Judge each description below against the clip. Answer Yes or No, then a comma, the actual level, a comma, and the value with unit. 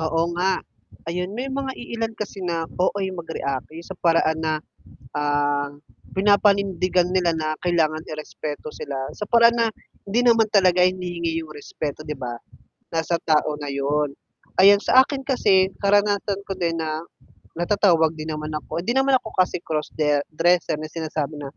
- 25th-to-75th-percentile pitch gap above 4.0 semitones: Yes, average, 4.4 semitones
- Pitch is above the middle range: No, medium, 170 Hz